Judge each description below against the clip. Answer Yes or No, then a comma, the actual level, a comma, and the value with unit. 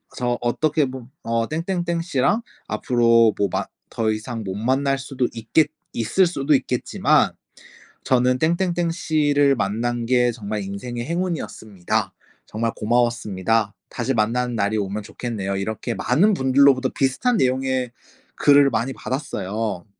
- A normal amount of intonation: Yes, average, 4.1 semitones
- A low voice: Yes, low, 125 Hz